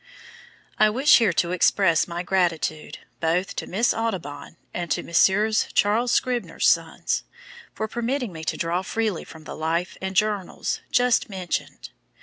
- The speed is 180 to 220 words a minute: No, average, 145 wpm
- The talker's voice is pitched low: No, high, 190 Hz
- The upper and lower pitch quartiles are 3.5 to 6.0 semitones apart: Yes, average, 4.7 semitones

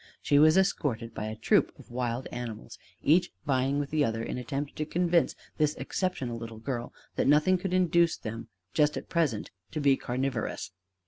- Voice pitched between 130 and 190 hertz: Yes, medium, 140 Hz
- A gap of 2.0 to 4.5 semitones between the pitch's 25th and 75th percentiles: No, average, 5.0 semitones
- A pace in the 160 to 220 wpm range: Yes, average, 180 wpm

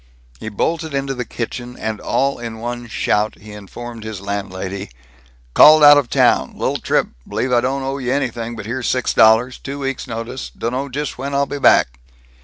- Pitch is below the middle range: Yes, low, 120 Hz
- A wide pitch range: No, average, 3.7 semitones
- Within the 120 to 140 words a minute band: No, average, 185 wpm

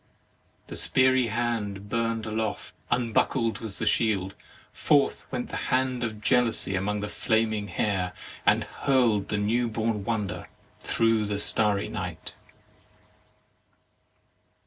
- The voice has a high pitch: No, low, 110 Hz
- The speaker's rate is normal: No, slow, 125 wpm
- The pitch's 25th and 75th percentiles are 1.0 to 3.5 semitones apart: Yes, narrow, 2.4 semitones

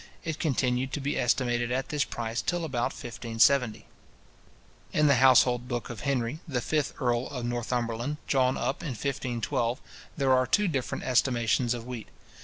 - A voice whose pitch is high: No, low, 125 Hz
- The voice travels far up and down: No, narrow, 2.5 semitones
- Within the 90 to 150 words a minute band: No, average, 160 wpm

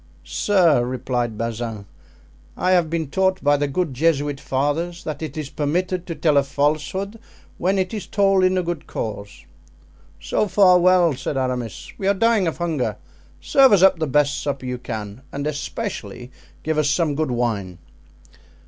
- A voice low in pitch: No, medium, 150 Hz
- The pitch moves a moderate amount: No, wide, 5.9 semitones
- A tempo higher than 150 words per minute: Yes, average, 170 wpm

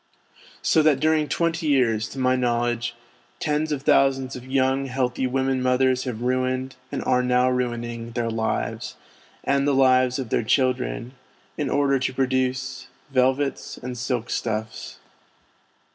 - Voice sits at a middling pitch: No, low, 130 Hz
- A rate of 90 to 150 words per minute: Yes, average, 145 wpm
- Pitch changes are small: Yes, narrow, 1.5 semitones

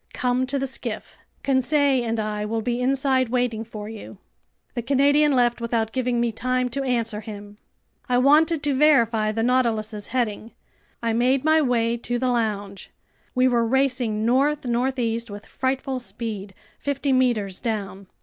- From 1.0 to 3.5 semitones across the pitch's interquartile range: Yes, average, 2.8 semitones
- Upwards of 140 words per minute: Yes, average, 160 wpm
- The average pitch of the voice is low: No, high, 240 Hz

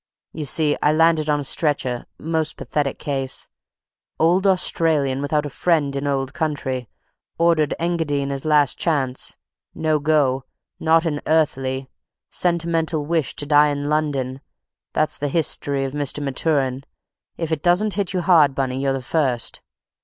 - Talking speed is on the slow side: Yes, slow, 130 wpm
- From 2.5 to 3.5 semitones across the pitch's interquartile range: Yes, average, 2.8 semitones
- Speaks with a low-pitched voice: No, medium, 150 Hz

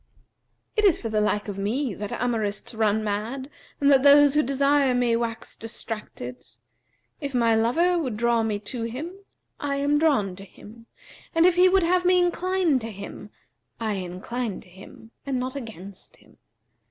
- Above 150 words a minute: Yes, average, 175 wpm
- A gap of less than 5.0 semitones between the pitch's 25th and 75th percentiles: No, average, 5.3 semitones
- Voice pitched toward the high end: Yes, high, 240 Hz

